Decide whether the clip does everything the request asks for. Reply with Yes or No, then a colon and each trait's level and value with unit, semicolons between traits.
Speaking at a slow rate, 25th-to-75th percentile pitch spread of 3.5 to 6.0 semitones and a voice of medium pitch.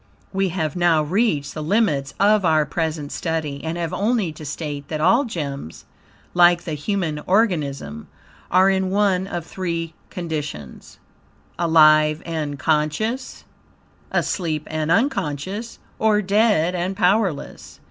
Yes: slow, 125 wpm; average, 4.2 semitones; medium, 170 Hz